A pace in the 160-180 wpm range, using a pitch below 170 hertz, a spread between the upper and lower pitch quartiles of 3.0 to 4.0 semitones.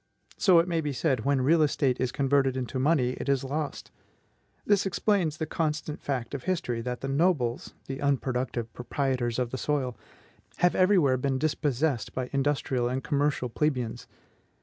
Yes: average, 170 wpm; medium, 140 Hz; average, 3.3 semitones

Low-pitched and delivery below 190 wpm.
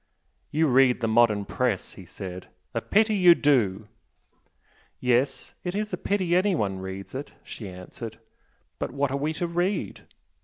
Yes: low, 125 Hz; average, 150 wpm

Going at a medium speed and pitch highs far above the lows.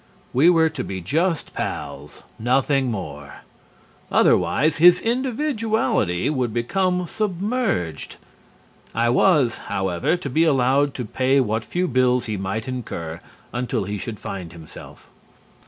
No: slow, 125 wpm; wide, 8.1 semitones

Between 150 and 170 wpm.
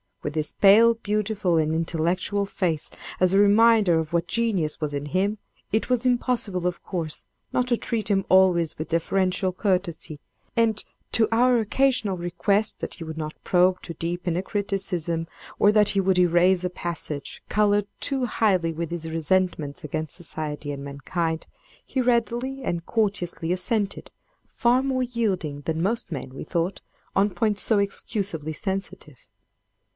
Yes: average, 155 wpm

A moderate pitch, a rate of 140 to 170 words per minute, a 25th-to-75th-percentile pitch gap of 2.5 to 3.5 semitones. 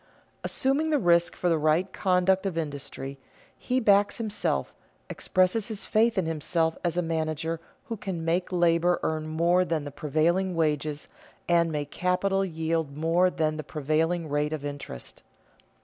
Yes: medium, 165 Hz; average, 160 wpm; average, 2.9 semitones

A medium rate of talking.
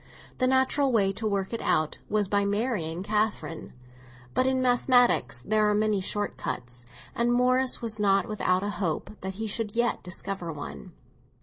Yes: average, 170 wpm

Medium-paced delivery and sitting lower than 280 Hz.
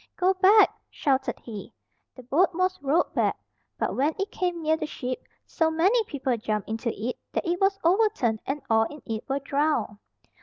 No: average, 185 wpm; very high, 300 Hz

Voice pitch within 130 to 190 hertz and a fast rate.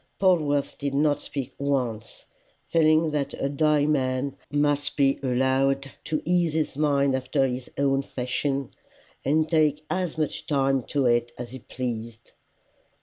No: medium, 140 Hz; average, 145 wpm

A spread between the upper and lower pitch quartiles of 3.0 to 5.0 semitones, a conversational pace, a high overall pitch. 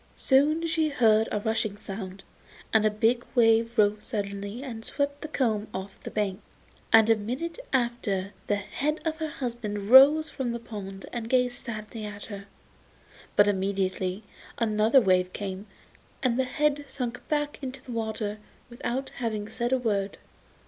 Yes: average, 3.9 semitones; average, 160 wpm; high, 225 Hz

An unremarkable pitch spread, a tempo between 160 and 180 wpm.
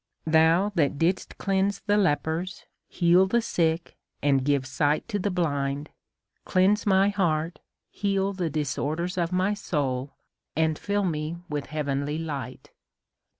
No: average, 4.5 semitones; average, 140 wpm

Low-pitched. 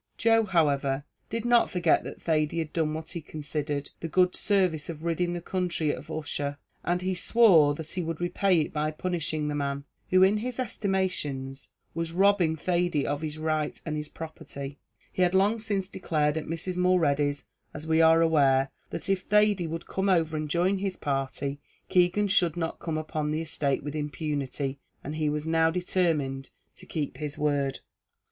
No: medium, 160 Hz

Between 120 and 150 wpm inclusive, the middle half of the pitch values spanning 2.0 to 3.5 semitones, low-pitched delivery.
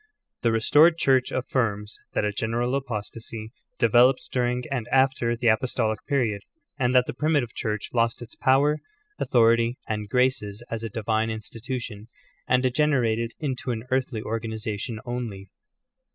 Yes: average, 145 wpm; narrow, 2.6 semitones; low, 120 Hz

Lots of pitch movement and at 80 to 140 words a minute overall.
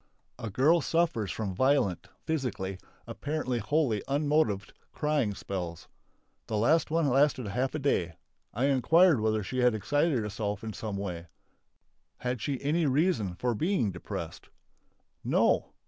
Yes: wide, 6.3 semitones; slow, 135 wpm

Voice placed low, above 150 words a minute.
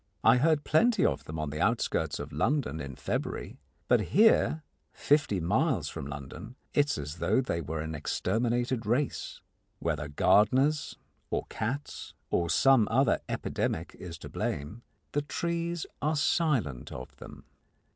No: low, 115 Hz; average, 145 wpm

